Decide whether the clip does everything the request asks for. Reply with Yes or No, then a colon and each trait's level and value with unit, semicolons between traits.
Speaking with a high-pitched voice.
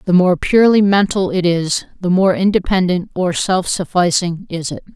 No: medium, 180 Hz